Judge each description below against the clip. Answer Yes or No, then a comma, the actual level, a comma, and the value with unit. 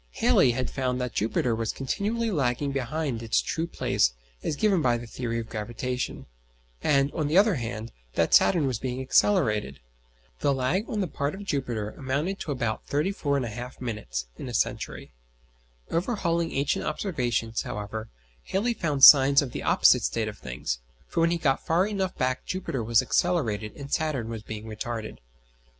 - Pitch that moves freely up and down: Yes, wide, 6.0 semitones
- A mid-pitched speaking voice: No, low, 130 Hz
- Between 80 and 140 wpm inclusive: No, average, 170 wpm